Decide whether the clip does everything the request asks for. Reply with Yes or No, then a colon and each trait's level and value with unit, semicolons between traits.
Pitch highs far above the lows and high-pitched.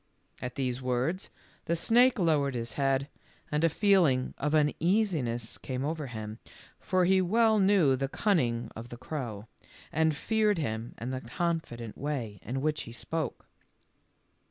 No: wide, 5.9 semitones; medium, 145 Hz